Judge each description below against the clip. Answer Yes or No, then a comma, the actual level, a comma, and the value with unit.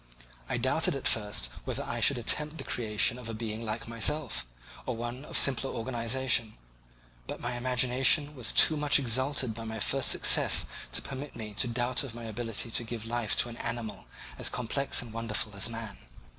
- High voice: No, low, 120 Hz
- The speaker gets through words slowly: No, average, 185 wpm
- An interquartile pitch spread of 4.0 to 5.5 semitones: No, narrow, 2.6 semitones